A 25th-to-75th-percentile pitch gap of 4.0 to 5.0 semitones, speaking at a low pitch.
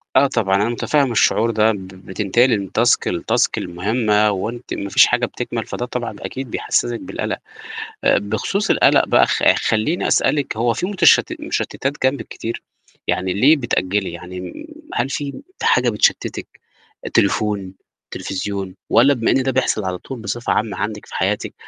Yes: average, 4.3 semitones; low, 110 Hz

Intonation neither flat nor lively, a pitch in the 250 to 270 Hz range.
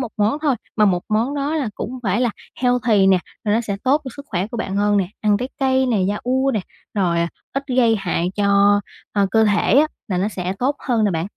No: average, 4.3 semitones; high, 215 Hz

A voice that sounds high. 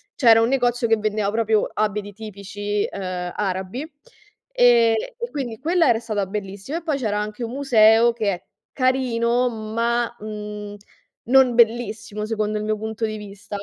Yes: high, 220 Hz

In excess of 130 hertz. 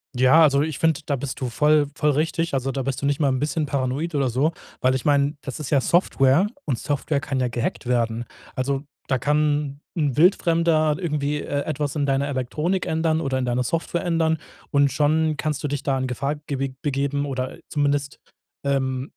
Yes: medium, 140 Hz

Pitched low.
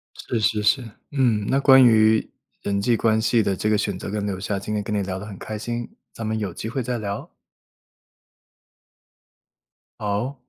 Yes: low, 110 Hz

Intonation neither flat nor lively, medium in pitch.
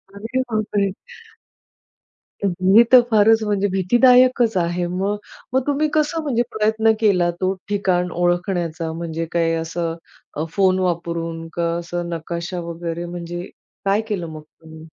Yes: average, 3.9 semitones; medium, 180 Hz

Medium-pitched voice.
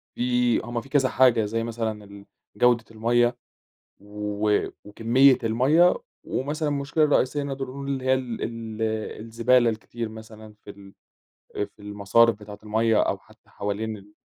No: low, 115 Hz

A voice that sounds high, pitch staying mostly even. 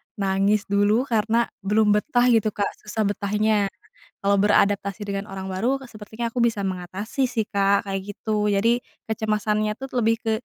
Yes: high, 210 Hz; narrow, 2.1 semitones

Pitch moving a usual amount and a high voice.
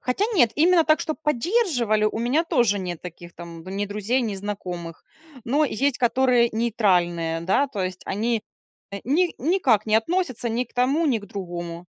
No: wide, 6.1 semitones; high, 230 Hz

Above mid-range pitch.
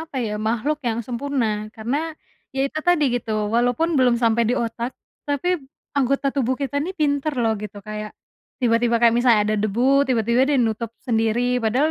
Yes: high, 240 Hz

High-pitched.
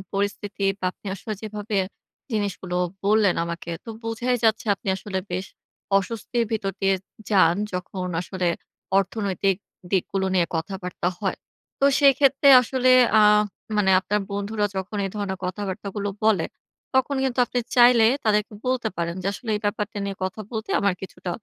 Yes: high, 205 Hz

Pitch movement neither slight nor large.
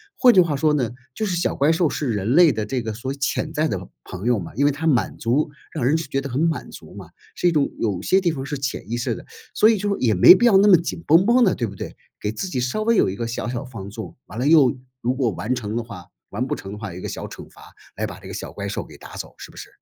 No: wide, 6.3 semitones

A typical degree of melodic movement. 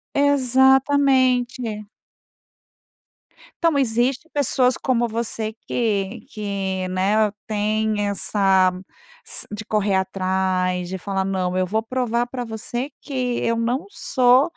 Yes: average, 4.5 semitones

